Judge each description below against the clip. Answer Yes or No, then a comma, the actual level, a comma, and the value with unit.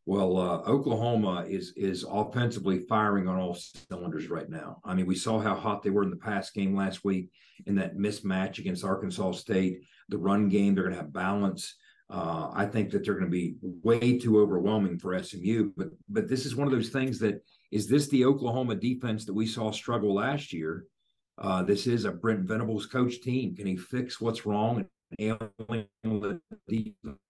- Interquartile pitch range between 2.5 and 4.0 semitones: Yes, average, 3.6 semitones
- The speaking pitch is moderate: No, low, 105 Hz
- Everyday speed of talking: Yes, average, 190 wpm